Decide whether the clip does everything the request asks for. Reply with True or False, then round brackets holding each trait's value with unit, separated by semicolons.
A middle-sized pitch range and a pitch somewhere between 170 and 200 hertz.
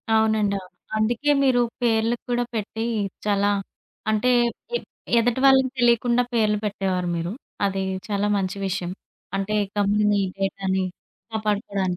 False (3.2 semitones; 210 Hz)